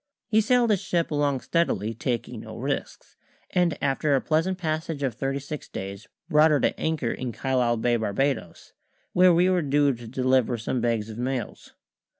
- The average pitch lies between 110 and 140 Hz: Yes, low, 135 Hz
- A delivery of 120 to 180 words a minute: Yes, average, 175 wpm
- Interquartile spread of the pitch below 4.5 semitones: No, average, 5.1 semitones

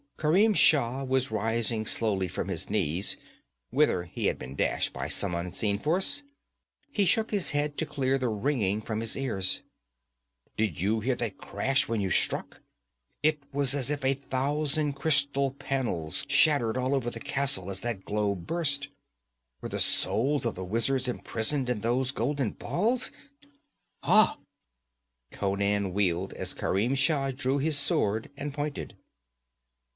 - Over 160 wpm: No, average, 150 wpm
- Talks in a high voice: No, low, 130 Hz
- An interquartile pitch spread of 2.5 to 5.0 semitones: No, wide, 5.4 semitones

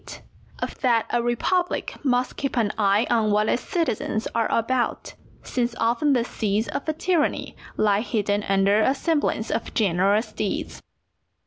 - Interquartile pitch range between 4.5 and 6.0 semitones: No, average, 3.5 semitones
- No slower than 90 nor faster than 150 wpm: Yes, average, 145 wpm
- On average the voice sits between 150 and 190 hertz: No, high, 230 Hz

